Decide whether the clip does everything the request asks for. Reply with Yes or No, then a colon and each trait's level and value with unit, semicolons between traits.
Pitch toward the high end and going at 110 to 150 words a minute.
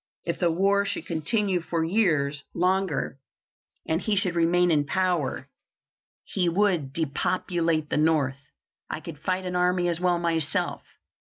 No: medium, 170 Hz; average, 145 wpm